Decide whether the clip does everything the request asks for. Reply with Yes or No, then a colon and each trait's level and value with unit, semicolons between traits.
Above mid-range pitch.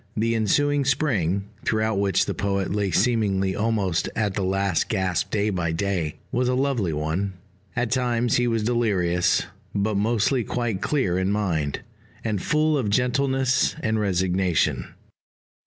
No: low, 105 Hz